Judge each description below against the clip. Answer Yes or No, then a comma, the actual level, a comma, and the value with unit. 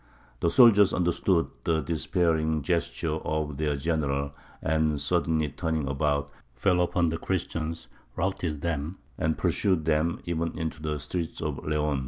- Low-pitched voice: Yes, very low, 80 Hz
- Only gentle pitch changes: Yes, narrow, 2.2 semitones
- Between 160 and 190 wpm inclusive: No, average, 140 wpm